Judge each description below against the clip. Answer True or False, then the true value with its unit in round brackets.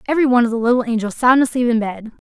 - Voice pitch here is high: True (240 Hz)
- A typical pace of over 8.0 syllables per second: True (8.2 syllables/s)